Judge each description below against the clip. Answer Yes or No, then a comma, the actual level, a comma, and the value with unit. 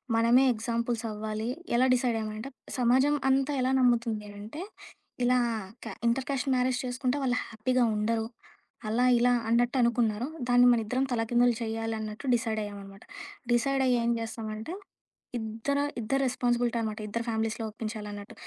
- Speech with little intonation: Yes, narrow, 2.3 semitones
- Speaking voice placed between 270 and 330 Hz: No, high, 235 Hz